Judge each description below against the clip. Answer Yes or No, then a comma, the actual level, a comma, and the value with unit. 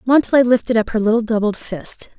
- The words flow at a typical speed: Yes, average, 195 wpm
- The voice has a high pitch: Yes, high, 230 Hz